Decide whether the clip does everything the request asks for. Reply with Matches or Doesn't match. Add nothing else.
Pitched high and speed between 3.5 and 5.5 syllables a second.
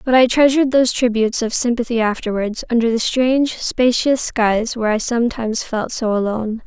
Doesn't match